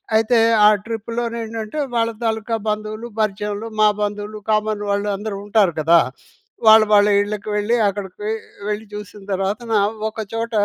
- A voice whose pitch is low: No, high, 215 Hz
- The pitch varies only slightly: Yes, narrow, 1.5 semitones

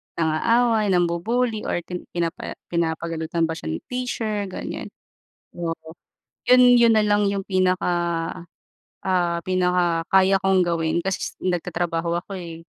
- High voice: No, medium, 180 Hz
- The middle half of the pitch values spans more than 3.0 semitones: Yes, average, 3.4 semitones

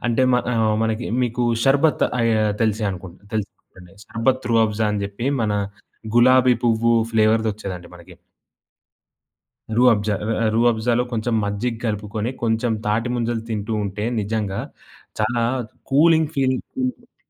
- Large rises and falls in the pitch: No, narrow, 2.4 semitones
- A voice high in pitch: No, low, 115 Hz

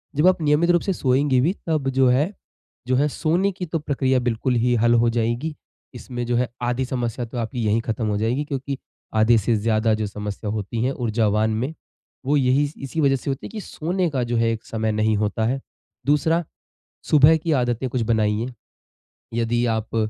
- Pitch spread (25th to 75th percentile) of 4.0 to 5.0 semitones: Yes, average, 4.4 semitones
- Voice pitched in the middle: No, low, 125 Hz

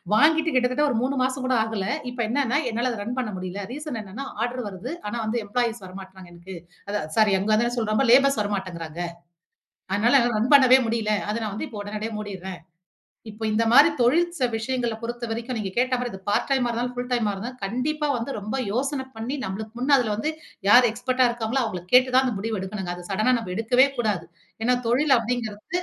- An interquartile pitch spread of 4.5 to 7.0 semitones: No, average, 3.4 semitones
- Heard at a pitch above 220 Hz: Yes, high, 235 Hz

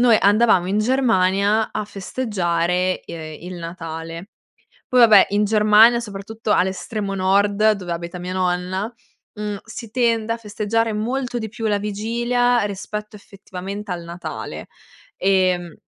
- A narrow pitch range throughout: No, average, 3.3 semitones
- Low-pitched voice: No, high, 205 Hz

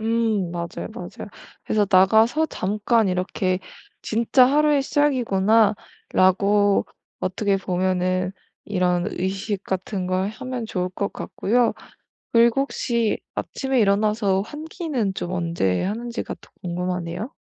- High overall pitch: Yes, high, 205 Hz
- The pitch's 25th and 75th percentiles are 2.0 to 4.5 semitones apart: Yes, average, 4.1 semitones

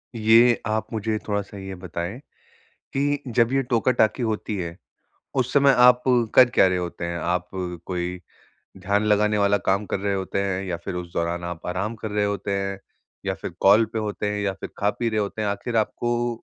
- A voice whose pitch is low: Yes, low, 105 Hz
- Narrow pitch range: No, average, 3.2 semitones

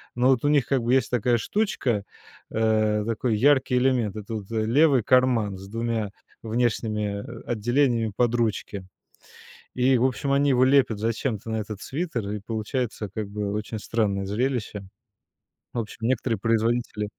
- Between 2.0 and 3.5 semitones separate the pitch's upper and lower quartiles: Yes, average, 3.1 semitones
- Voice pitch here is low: Yes, low, 115 Hz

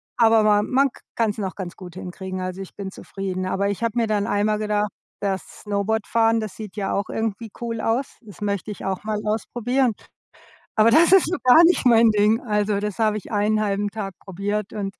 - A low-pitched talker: No, high, 210 Hz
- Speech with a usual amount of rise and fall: No, narrow, 2.1 semitones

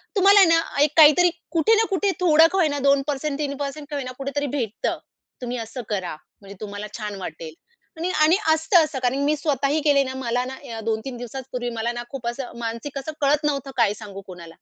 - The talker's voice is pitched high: Yes, very high, 275 Hz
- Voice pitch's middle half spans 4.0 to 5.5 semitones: Yes, average, 4.6 semitones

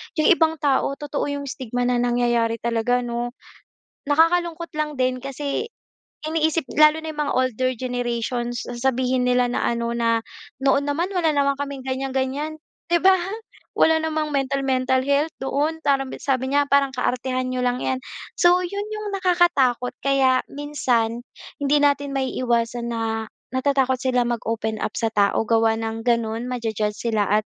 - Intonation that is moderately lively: Yes, average, 3.3 semitones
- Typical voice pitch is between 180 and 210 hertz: No, very high, 260 Hz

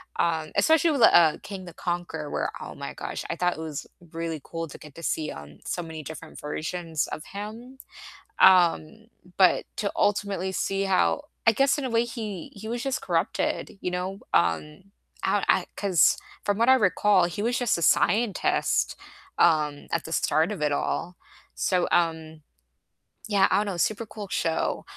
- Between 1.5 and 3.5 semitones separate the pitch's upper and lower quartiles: No, average, 4.5 semitones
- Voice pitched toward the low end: No, medium, 180 Hz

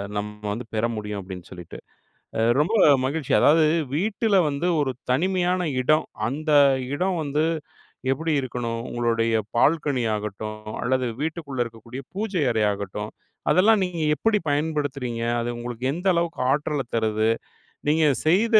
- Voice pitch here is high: No, low, 135 Hz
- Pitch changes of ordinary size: No, wide, 6.1 semitones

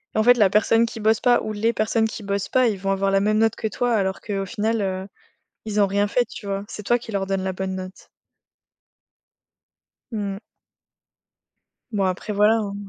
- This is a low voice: No, high, 205 Hz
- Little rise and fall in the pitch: Yes, narrow, 2.3 semitones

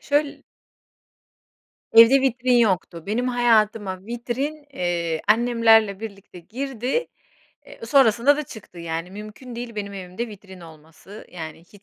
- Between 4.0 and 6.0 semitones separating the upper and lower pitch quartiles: Yes, average, 4.6 semitones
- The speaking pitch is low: No, high, 220 Hz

